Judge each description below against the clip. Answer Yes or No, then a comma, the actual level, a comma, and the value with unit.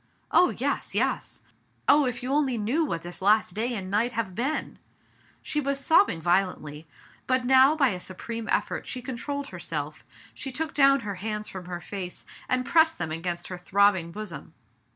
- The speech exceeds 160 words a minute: Yes, average, 185 wpm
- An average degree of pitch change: No, wide, 6.8 semitones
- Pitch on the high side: Yes, high, 225 Hz